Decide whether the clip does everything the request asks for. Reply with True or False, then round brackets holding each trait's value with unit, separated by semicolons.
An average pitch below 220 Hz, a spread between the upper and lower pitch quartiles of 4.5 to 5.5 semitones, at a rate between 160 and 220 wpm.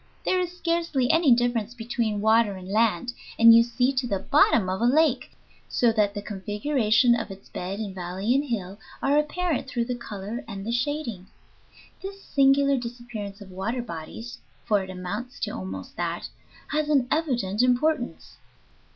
False (235 Hz; 4.9 semitones; 170 wpm)